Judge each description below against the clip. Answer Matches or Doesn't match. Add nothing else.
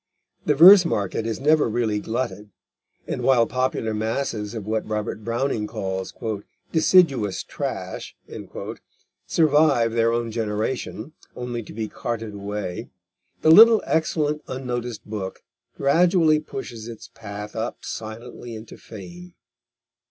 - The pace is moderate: Doesn't match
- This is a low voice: Matches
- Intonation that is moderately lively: Matches